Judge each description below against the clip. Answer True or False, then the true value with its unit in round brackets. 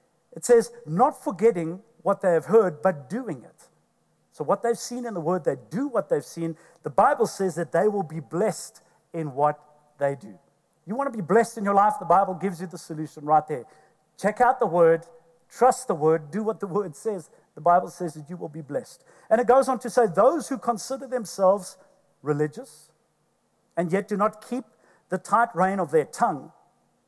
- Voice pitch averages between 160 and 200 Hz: True (190 Hz)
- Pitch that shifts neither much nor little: False (6.0 semitones)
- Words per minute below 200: False (205 wpm)